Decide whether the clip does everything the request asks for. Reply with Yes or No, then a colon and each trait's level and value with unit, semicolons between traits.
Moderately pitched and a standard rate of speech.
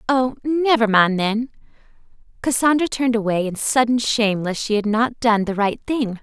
No: high, 230 Hz; average, 175 wpm